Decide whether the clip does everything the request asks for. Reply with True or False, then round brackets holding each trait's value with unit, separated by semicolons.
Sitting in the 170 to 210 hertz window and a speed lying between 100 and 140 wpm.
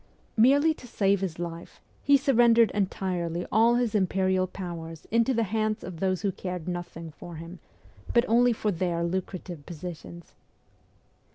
False (190 Hz; 150 wpm)